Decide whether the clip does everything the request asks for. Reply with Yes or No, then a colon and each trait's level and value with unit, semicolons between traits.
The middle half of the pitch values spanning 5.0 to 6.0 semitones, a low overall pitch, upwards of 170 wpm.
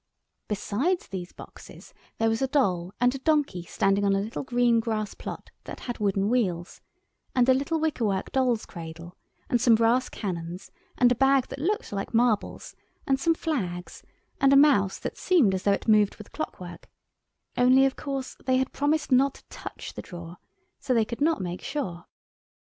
No: wide, 5.5 semitones; high, 235 Hz; average, 180 wpm